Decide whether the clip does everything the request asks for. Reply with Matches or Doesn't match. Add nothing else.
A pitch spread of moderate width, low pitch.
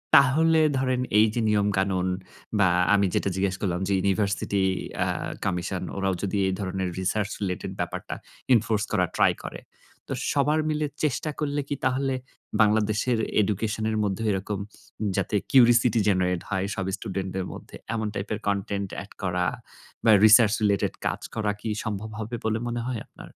Matches